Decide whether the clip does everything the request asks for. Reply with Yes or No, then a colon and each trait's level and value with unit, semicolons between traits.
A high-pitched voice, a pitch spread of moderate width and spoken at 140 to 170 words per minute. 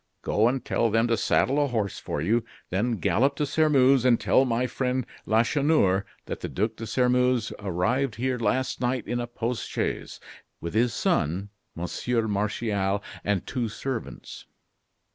No: low, 120 Hz; average, 3.6 semitones; average, 160 wpm